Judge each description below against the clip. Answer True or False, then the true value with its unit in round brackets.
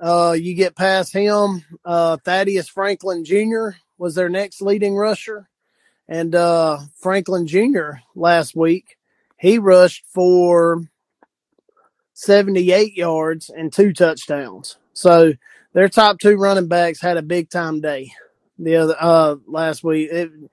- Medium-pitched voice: True (175 Hz)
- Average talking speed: False (130 wpm)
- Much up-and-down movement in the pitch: False (3.1 semitones)